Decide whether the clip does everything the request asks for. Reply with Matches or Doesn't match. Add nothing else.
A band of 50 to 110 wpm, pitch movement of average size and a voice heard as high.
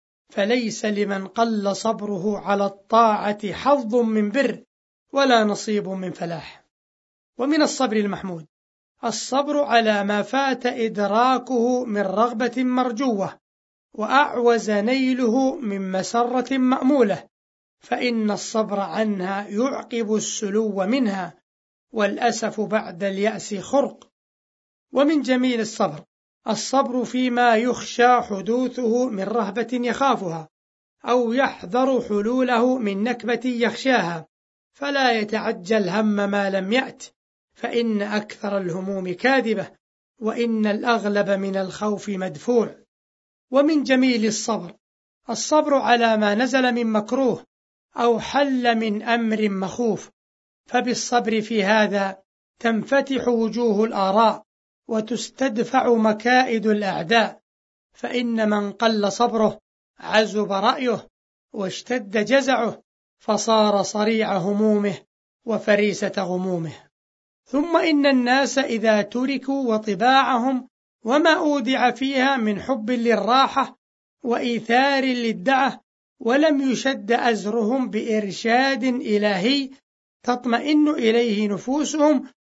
Matches